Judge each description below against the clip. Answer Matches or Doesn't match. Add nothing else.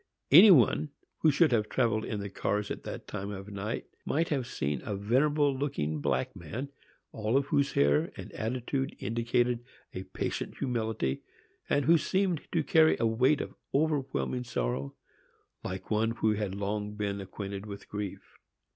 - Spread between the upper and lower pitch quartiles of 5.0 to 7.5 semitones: Matches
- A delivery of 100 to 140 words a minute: Doesn't match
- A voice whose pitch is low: Matches